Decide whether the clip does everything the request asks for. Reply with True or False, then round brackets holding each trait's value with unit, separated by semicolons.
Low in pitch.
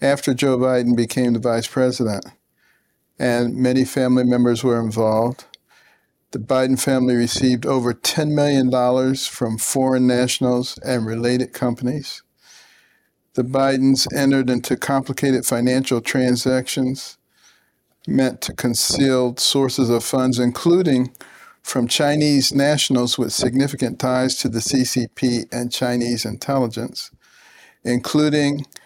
True (130 Hz)